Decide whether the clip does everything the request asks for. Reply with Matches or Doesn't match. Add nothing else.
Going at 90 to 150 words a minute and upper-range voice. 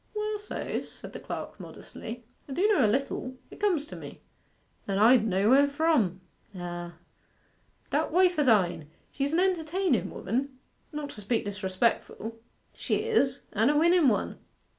Doesn't match